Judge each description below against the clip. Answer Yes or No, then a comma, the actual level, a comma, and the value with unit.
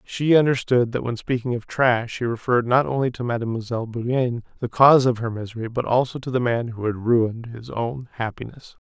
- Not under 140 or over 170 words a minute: No, fast, 205 wpm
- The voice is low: Yes, low, 120 Hz